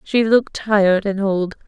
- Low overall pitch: No, high, 200 Hz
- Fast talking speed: No, average, 180 wpm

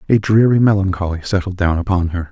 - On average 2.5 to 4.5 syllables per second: No, 6.2 syllables/s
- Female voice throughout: No, male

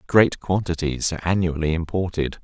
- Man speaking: Yes, male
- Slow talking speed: Yes, slow, 125 wpm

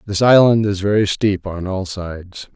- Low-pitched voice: Yes, low, 100 Hz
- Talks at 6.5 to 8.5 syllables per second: No, 4.6 syllables/s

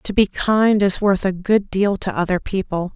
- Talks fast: Yes, fast, 225 wpm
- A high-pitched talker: Yes, high, 195 Hz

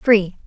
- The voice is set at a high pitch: Yes, high, 205 Hz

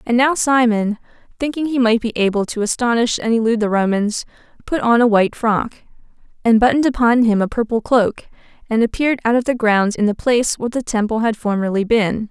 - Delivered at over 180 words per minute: Yes, average, 200 wpm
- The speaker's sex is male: No, female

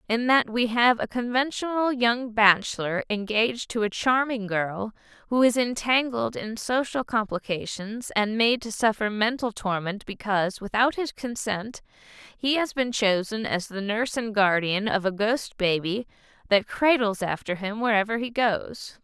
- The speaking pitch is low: No, high, 220 Hz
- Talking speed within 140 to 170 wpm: Yes, average, 155 wpm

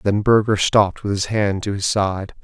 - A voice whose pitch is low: Yes, low, 100 Hz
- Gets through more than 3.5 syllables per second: Yes, 4.8 syllables/s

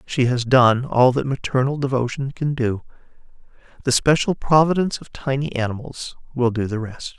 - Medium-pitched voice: No, low, 130 Hz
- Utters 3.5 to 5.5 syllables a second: Yes, 5.1 syllables/s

